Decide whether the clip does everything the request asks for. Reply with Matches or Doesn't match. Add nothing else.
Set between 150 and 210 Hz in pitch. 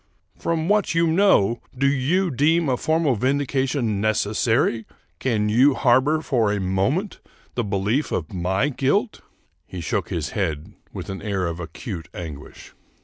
Doesn't match